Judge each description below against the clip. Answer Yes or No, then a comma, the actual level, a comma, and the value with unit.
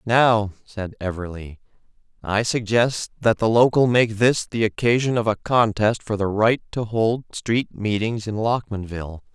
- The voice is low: Yes, low, 110 Hz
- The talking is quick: No, average, 155 wpm